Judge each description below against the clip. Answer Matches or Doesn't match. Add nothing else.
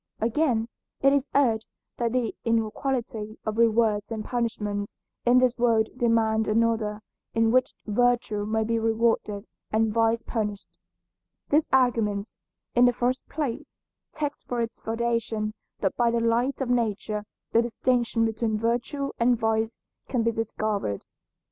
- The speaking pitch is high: Matches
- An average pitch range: Doesn't match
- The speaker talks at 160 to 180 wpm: Doesn't match